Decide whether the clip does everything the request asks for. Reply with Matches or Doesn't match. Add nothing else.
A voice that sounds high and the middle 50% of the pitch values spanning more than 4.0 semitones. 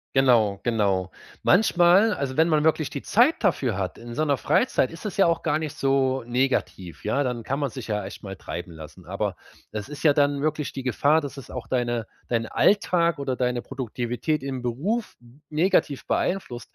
Doesn't match